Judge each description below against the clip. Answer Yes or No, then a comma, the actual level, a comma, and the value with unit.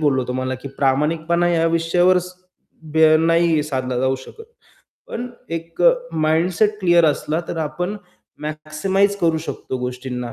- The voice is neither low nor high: Yes, medium, 160 Hz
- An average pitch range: Yes, average, 3.7 semitones